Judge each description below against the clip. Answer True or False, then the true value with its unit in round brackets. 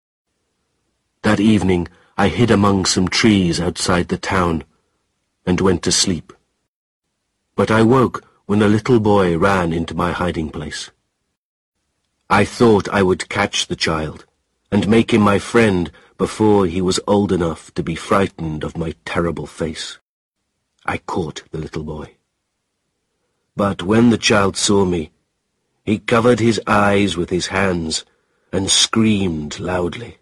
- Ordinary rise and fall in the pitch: True (3.7 semitones)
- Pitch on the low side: True (95 Hz)